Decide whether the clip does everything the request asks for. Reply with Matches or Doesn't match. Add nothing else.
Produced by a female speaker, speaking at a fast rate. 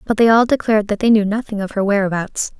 Matches